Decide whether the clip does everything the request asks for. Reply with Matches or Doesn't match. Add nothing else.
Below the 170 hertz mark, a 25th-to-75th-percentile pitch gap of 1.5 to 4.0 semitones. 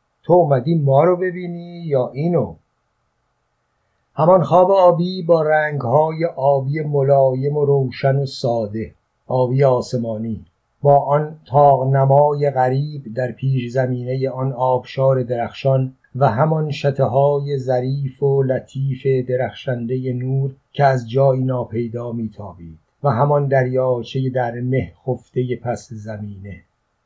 Matches